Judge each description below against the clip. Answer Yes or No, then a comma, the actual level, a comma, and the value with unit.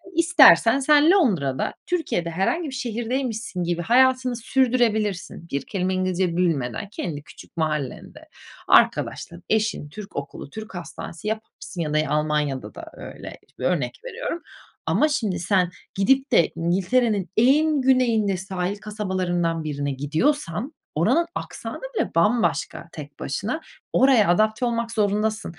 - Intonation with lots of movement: Yes, wide, 6.9 semitones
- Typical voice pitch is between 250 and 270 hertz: No, high, 205 Hz